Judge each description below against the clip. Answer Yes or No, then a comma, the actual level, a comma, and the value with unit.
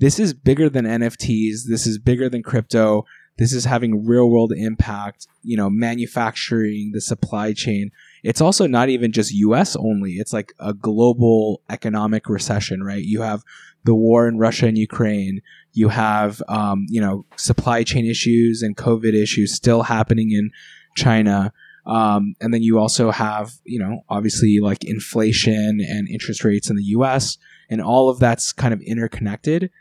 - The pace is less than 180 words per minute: Yes, average, 165 wpm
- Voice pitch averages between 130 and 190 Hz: No, low, 110 Hz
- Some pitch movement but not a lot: No, narrow, 2.0 semitones